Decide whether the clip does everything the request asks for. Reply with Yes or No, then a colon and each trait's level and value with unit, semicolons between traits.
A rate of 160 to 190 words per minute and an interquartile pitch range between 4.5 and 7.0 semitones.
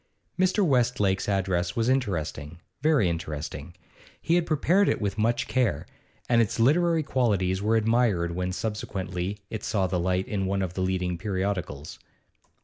No: average, 150 wpm; average, 5.0 semitones